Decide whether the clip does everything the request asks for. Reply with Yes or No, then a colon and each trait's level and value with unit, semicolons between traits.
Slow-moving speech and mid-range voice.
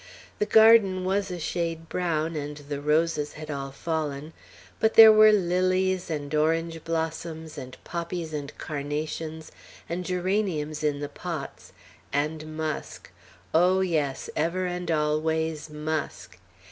Yes: slow, 130 wpm; medium, 160 Hz